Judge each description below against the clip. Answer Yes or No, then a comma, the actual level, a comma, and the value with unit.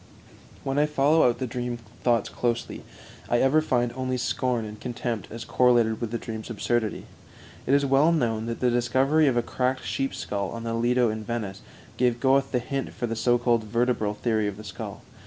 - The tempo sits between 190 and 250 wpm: Yes, average, 200 wpm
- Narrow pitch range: Yes, narrow, 2.3 semitones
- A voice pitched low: Yes, low, 120 Hz